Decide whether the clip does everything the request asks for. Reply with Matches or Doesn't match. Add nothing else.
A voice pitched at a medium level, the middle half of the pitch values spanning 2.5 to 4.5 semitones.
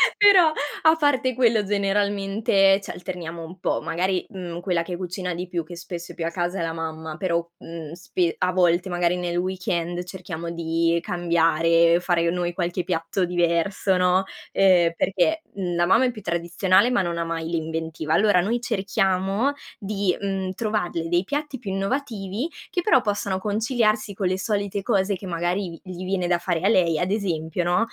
Matches